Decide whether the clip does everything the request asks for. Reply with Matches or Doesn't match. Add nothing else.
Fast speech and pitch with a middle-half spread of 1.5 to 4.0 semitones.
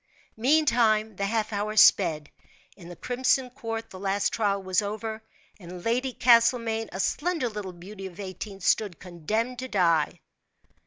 Doesn't match